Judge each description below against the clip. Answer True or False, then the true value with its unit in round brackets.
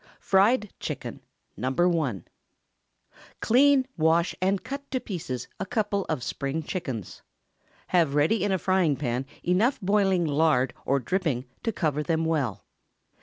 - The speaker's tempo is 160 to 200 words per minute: False (135 wpm)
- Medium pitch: True (170 Hz)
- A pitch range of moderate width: False (6.0 semitones)